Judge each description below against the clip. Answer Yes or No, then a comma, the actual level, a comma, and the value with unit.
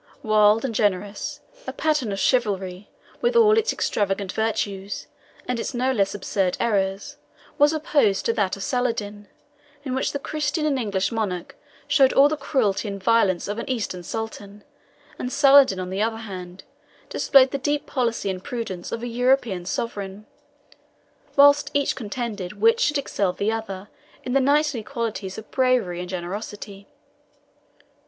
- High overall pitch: Yes, high, 225 Hz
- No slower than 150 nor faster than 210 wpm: Yes, average, 155 wpm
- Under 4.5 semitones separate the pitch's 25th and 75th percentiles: No, average, 5.2 semitones